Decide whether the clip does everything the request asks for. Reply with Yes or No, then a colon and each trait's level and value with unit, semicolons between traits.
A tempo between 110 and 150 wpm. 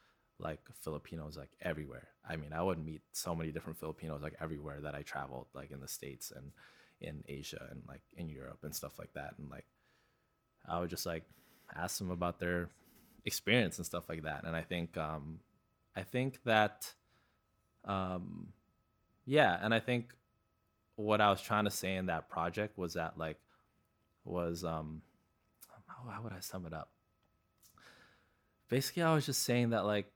No: average, 175 wpm